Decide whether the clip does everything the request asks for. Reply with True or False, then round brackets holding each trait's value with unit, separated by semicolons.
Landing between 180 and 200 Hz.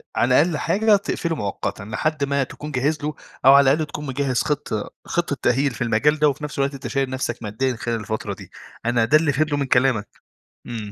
False (140 Hz)